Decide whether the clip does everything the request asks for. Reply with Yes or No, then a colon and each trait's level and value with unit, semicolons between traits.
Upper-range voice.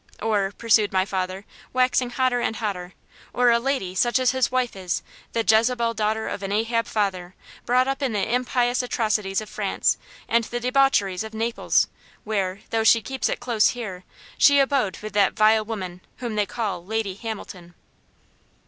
Yes: high, 220 Hz